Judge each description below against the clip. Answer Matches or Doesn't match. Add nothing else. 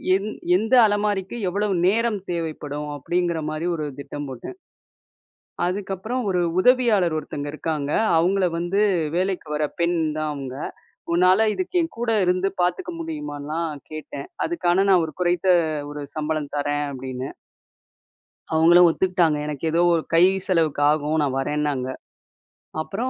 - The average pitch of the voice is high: Doesn't match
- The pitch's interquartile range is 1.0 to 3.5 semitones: Doesn't match